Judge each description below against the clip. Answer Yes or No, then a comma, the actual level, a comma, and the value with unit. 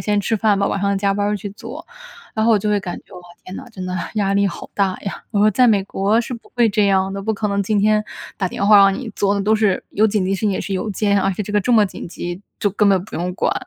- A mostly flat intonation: Yes, narrow, 1.6 semitones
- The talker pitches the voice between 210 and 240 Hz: No, high, 200 Hz